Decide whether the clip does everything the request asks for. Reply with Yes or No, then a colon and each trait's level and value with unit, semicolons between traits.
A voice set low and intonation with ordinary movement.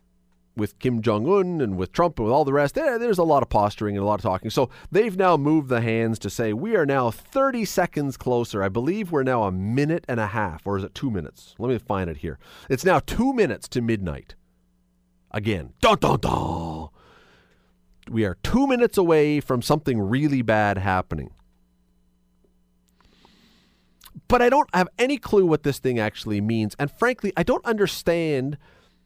No: low, 115 Hz; wide, 8.9 semitones